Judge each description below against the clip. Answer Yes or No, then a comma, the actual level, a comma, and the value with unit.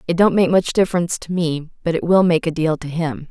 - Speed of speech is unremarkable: No, fast, 270 wpm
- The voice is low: No, medium, 170 Hz